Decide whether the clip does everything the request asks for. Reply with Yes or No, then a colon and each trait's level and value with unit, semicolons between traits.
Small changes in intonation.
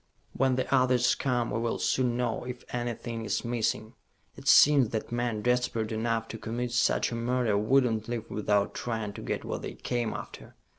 Yes: narrow, 1.8 semitones